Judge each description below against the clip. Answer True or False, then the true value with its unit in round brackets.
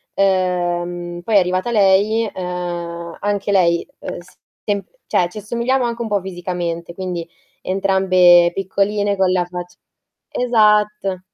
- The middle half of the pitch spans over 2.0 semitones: True (2.7 semitones)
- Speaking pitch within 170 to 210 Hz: True (185 Hz)